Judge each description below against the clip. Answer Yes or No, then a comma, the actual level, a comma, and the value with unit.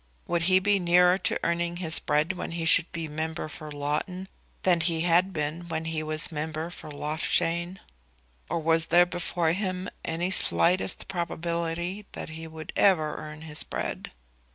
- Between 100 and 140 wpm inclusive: No, average, 165 wpm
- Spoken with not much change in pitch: Yes, narrow, 2.0 semitones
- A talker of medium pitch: Yes, medium, 170 Hz